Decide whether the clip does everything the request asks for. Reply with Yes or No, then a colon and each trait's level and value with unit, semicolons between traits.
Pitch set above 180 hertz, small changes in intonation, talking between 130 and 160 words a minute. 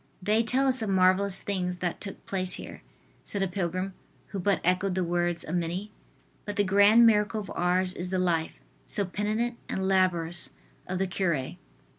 No: high, 190 Hz; narrow, 2.2 semitones; average, 180 wpm